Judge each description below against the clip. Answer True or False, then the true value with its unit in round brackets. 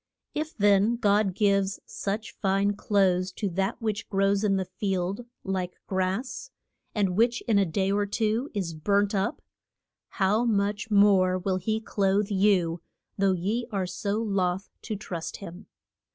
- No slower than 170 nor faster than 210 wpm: False (150 wpm)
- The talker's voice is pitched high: True (200 Hz)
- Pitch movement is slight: True (1.9 semitones)